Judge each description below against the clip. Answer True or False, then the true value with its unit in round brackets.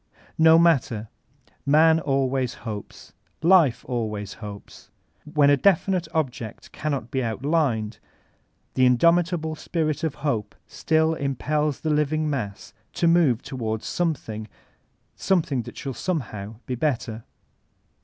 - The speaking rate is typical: False (125 wpm)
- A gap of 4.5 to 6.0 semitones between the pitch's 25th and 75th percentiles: True (5.4 semitones)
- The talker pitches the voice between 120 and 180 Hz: True (140 Hz)